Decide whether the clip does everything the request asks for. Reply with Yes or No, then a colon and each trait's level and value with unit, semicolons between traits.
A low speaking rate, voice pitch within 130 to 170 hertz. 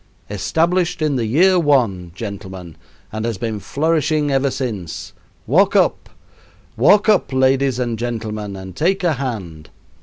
No: slow, 130 wpm; low, 120 Hz